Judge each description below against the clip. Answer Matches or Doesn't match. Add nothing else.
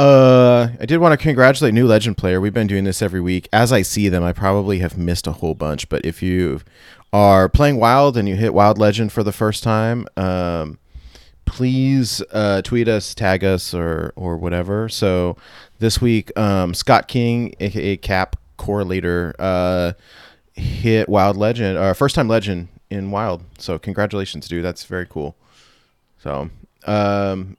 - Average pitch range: Matches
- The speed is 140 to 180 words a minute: Matches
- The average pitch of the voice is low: Matches